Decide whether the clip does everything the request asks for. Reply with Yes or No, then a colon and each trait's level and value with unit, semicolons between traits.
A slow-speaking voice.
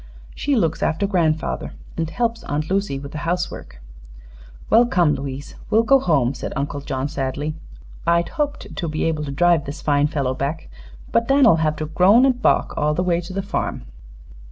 No: average, 185 wpm